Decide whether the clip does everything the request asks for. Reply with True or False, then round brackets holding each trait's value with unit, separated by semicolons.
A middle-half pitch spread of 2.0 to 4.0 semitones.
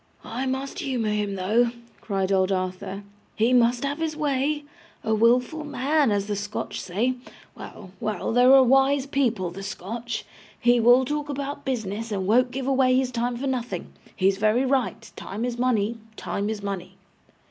False (4.4 semitones)